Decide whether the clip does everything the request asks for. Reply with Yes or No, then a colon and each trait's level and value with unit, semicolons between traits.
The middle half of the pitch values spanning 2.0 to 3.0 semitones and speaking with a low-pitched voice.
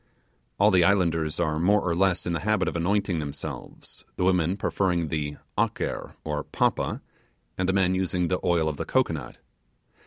Yes: average, 2.7 semitones; very low, 90 Hz